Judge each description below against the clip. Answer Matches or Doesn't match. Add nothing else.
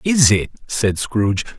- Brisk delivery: Doesn't match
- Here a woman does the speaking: Doesn't match